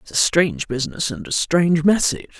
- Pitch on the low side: No, medium, 170 Hz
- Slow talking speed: No, average, 200 wpm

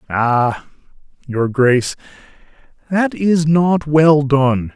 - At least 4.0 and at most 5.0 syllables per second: No, 3.0 syllables/s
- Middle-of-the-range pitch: Yes, medium, 145 Hz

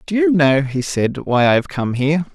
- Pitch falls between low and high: Yes, medium, 145 Hz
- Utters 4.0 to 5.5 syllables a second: Yes, 5.1 syllables/s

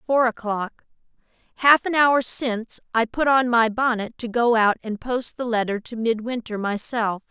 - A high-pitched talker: Yes, high, 235 Hz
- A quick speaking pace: No, average, 165 wpm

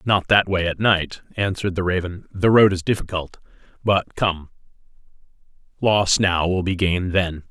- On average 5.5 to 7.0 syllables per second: No, 4.7 syllables/s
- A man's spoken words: Yes, male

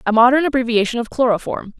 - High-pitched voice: Yes, high, 240 Hz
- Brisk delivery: No, average, 165 wpm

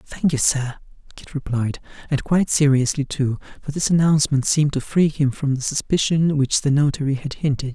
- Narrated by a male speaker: Yes, male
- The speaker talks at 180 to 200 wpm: Yes, average, 185 wpm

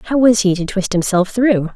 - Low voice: No, high, 205 Hz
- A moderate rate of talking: No, fast, 240 wpm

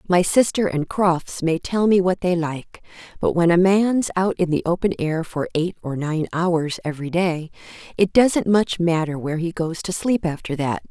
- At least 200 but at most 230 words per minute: Yes, fast, 205 wpm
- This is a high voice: No, medium, 175 Hz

